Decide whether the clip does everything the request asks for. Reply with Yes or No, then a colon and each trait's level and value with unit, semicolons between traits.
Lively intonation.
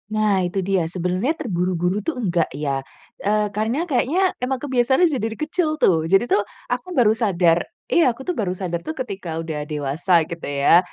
Yes: wide, 6.6 semitones